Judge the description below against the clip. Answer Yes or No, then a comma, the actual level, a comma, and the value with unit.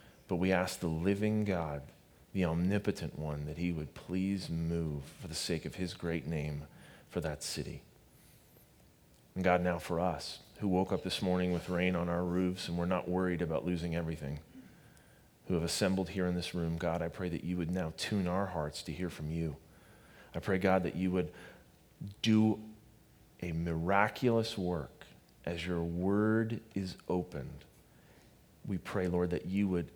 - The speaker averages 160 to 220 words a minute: Yes, average, 175 wpm